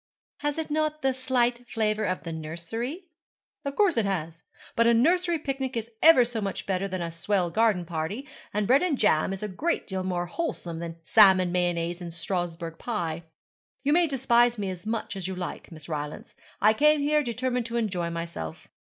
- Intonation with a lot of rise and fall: Yes, wide, 6.9 semitones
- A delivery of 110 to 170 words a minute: No, average, 195 wpm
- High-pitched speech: Yes, high, 210 Hz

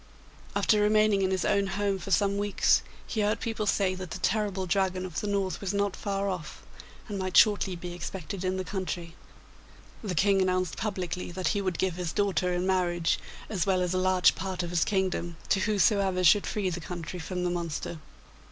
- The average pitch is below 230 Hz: Yes, medium, 185 Hz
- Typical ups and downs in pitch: No, narrow, 2.0 semitones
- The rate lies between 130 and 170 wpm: No, average, 200 wpm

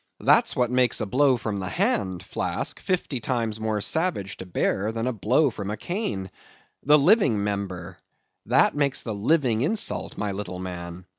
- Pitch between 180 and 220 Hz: No, low, 110 Hz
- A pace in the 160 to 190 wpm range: Yes, average, 165 wpm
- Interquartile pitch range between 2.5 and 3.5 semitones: No, wide, 5.5 semitones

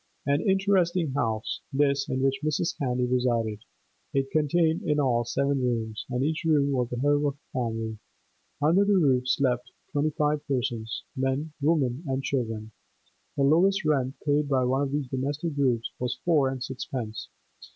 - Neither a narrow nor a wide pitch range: Yes, average, 3.1 semitones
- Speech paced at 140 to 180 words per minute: Yes, average, 165 wpm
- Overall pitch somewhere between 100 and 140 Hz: Yes, low, 135 Hz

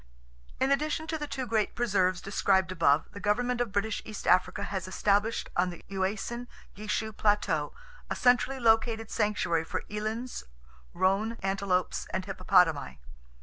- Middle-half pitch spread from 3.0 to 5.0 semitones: Yes, average, 3.7 semitones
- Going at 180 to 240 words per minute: No, average, 145 wpm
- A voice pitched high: Yes, high, 205 Hz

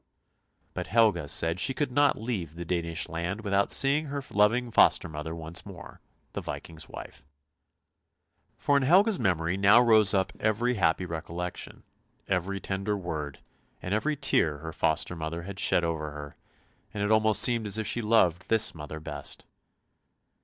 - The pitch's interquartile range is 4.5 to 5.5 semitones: Yes, average, 5.2 semitones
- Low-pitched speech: Yes, very low, 95 Hz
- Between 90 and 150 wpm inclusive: No, average, 165 wpm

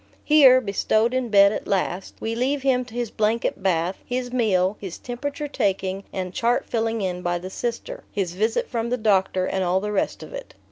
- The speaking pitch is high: Yes, high, 215 Hz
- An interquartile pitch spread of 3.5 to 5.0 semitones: Yes, average, 4.5 semitones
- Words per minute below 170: No, average, 200 wpm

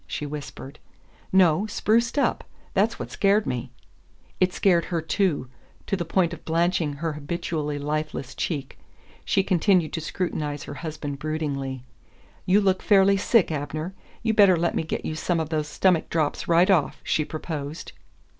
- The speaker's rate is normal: Yes, average, 160 wpm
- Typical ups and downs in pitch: Yes, average, 3.9 semitones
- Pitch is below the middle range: No, medium, 165 Hz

